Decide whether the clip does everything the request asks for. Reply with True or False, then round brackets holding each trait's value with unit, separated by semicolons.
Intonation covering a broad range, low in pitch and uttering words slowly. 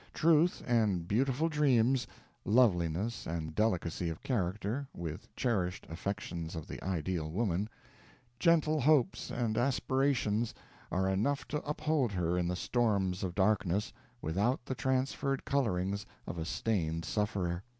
True (6.5 semitones; 105 Hz; 130 wpm)